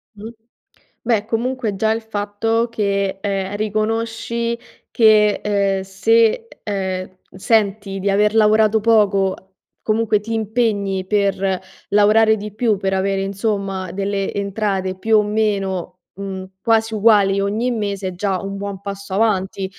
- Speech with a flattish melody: Yes, narrow, 2.1 semitones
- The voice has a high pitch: Yes, high, 205 Hz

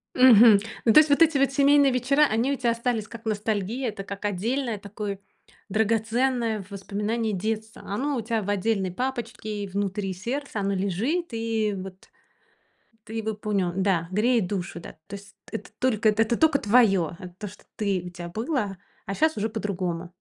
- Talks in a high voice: Yes, high, 215 Hz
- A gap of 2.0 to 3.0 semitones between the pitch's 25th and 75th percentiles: No, average, 3.5 semitones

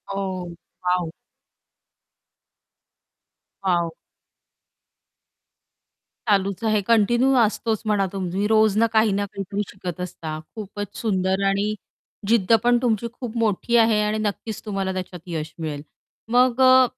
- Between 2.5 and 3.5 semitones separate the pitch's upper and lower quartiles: Yes, average, 3.1 semitones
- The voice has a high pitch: Yes, high, 205 Hz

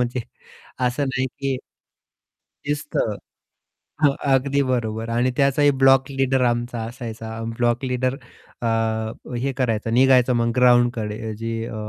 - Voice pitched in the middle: No, low, 125 Hz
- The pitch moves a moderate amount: No, narrow, 2.2 semitones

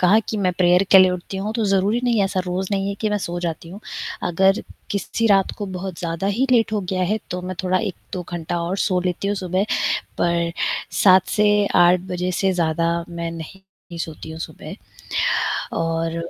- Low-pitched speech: No, medium, 185 Hz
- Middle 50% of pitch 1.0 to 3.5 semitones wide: Yes, narrow, 2.4 semitones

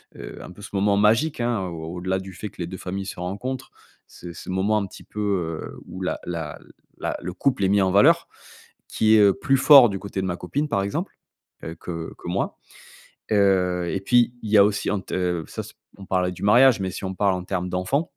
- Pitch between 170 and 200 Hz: No, very low, 95 Hz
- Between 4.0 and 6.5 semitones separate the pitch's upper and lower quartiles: No, average, 2.7 semitones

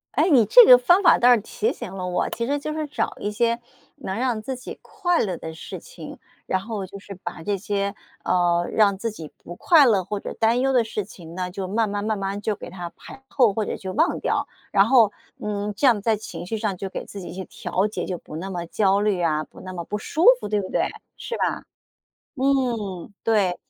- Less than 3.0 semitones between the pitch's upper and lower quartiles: No, average, 4.2 semitones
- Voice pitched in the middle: No, high, 205 Hz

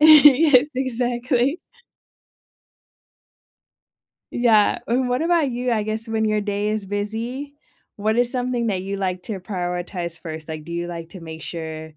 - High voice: Yes, high, 215 Hz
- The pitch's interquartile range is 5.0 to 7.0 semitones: Yes, wide, 5.6 semitones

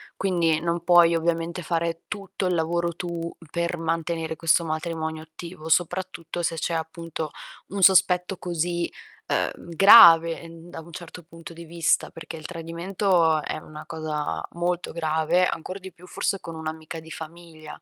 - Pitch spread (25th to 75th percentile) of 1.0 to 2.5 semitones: Yes, narrow, 1.4 semitones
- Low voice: No, medium, 170 Hz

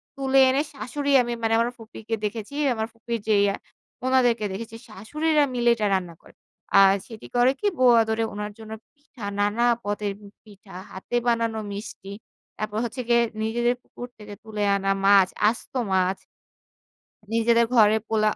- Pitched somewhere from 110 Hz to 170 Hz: No, high, 225 Hz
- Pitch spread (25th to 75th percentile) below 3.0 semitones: Yes, narrow, 2.4 semitones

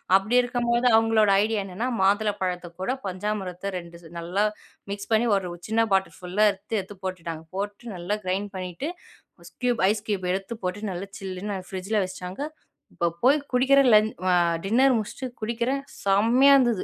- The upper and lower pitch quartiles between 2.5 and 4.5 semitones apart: Yes, average, 3.6 semitones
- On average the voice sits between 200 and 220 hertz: Yes, high, 205 Hz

